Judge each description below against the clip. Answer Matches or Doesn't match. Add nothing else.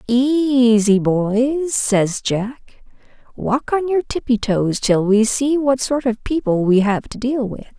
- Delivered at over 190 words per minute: Doesn't match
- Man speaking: Doesn't match